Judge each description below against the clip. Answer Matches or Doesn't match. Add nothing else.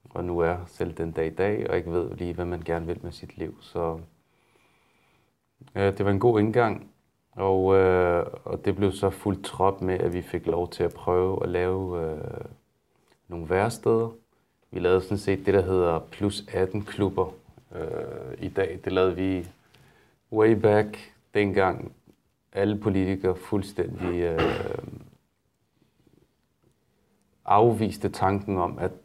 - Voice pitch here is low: Matches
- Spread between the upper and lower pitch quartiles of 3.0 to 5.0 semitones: Doesn't match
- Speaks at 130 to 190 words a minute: Matches